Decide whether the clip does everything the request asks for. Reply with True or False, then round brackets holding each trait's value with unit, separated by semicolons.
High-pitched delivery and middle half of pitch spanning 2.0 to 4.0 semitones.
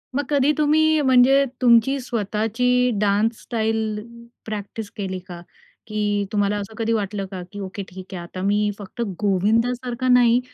True (220 Hz; 3.5 semitones)